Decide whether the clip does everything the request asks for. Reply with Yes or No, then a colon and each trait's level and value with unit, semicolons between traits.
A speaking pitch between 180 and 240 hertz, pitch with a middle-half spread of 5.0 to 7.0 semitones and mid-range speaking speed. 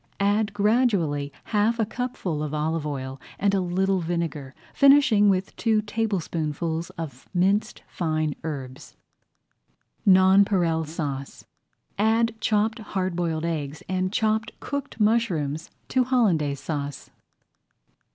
No: medium, 185 Hz; wide, 5.5 semitones; slow, 110 wpm